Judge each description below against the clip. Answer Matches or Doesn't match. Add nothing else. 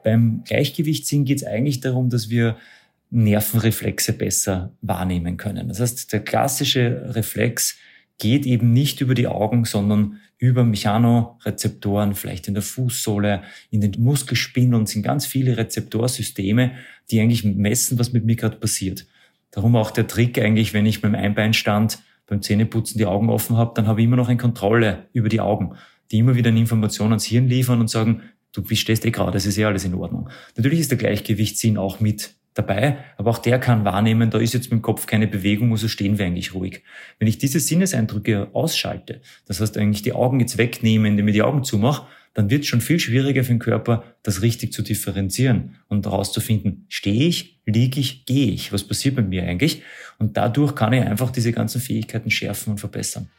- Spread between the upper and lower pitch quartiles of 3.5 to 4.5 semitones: Doesn't match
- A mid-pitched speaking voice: Doesn't match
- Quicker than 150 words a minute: Matches